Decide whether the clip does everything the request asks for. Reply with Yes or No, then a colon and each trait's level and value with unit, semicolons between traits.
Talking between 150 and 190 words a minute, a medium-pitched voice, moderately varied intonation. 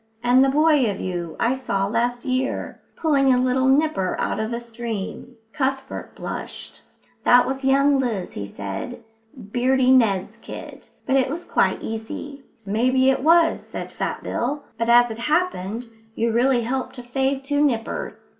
No: average, 165 wpm; very high, 250 Hz; average, 3.0 semitones